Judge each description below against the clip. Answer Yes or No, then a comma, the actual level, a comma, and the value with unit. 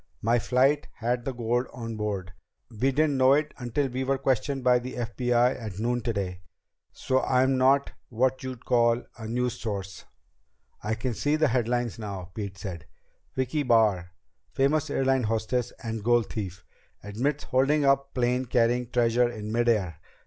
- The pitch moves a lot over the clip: No, average, 2.9 semitones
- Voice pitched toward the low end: Yes, low, 120 Hz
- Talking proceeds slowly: No, average, 165 wpm